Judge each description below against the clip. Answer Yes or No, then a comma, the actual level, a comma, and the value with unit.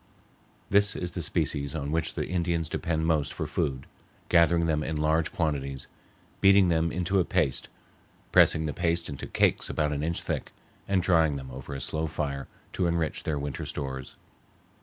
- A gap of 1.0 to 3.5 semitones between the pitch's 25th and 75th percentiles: Yes, average, 2.9 semitones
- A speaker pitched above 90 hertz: No, very low, 80 Hz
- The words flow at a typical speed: Yes, average, 175 wpm